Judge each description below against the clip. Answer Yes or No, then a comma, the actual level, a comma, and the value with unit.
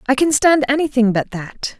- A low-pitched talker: No, very high, 260 Hz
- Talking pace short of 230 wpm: Yes, average, 200 wpm